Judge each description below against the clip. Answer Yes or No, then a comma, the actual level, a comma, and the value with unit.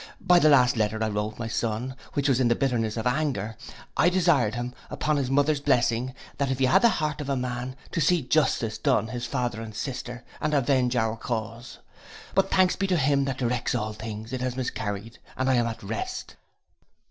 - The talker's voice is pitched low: Yes, low, 125 Hz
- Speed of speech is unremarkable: No, fast, 210 wpm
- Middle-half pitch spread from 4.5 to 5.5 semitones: No, average, 3.7 semitones